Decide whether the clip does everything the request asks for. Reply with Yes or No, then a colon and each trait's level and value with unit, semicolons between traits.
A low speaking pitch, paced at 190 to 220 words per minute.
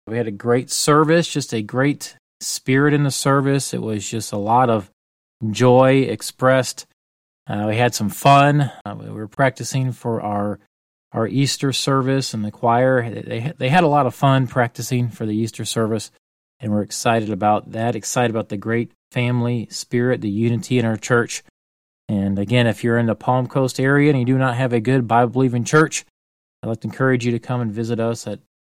Yes: low, 120 Hz; average, 200 wpm